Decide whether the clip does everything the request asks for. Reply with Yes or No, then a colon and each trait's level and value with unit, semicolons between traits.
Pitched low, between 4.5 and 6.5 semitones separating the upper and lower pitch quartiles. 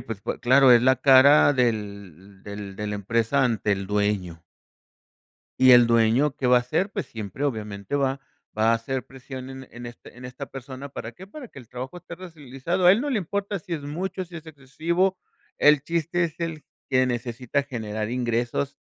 Yes: low, 130 Hz; average, 5.0 semitones